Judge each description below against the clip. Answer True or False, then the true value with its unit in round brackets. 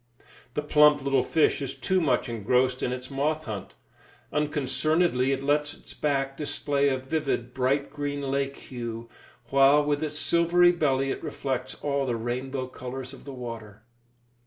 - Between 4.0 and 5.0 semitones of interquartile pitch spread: False (2.6 semitones)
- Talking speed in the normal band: True (160 wpm)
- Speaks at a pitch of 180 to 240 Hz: False (135 Hz)